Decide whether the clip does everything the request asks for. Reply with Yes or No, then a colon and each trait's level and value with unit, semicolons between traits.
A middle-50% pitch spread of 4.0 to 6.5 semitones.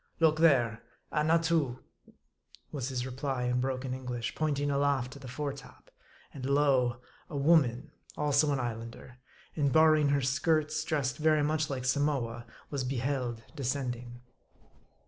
No: average, 3.1 semitones